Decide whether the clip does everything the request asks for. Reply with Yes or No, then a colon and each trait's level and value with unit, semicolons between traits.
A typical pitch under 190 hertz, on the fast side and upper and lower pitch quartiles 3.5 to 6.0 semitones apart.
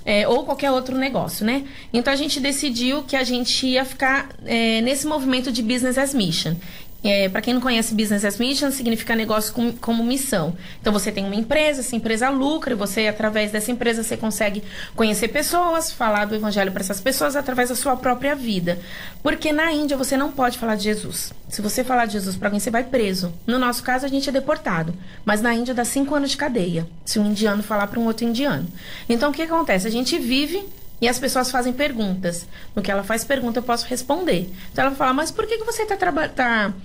No: high, 240 Hz; fast, 220 wpm; average, 4.4 semitones